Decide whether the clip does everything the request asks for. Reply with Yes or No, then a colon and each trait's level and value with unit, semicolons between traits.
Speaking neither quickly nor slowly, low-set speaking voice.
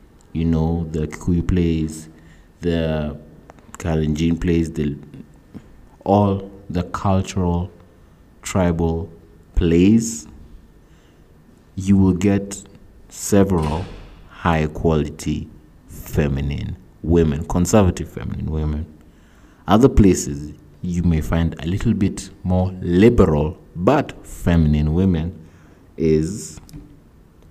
No: slow, 85 wpm; very low, 85 Hz